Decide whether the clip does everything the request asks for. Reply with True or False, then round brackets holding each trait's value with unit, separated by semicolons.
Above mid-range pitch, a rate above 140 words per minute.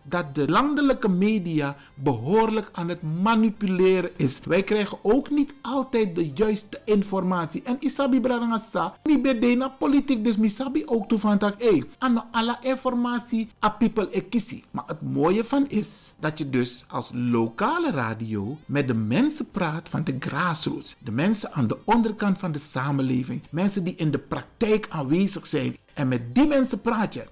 True (205 Hz; 155 wpm)